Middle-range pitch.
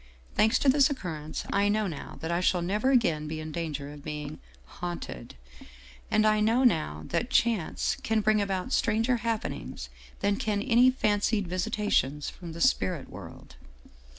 No: high, 200 Hz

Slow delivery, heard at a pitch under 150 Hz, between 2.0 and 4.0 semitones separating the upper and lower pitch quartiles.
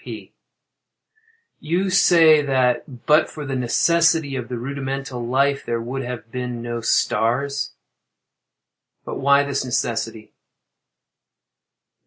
Yes: slow, 110 wpm; low, 135 Hz; average, 2.9 semitones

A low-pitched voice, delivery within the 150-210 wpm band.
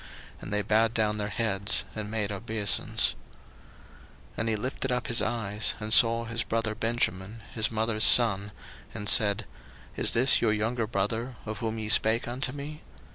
Yes: low, 110 Hz; average, 170 wpm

